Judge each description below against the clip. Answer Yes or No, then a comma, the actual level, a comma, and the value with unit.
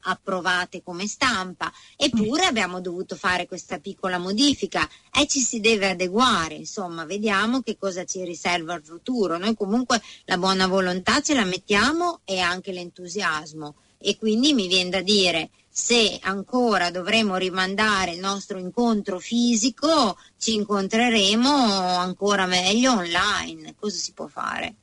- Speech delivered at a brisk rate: No, average, 140 wpm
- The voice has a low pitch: No, high, 195 Hz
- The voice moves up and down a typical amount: Yes, average, 3.7 semitones